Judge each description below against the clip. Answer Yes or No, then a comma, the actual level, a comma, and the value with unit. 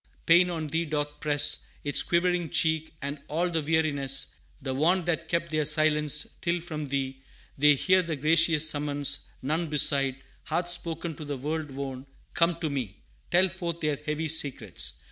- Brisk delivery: No, average, 165 wpm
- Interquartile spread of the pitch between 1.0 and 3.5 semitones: Yes, average, 2.7 semitones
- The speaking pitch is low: No, medium, 155 Hz